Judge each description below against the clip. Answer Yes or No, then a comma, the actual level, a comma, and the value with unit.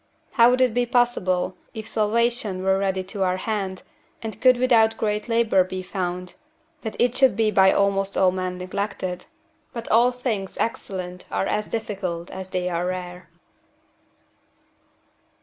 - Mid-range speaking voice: No, high, 195 Hz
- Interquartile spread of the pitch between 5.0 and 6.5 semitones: No, average, 3.7 semitones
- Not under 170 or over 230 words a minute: No, average, 150 wpm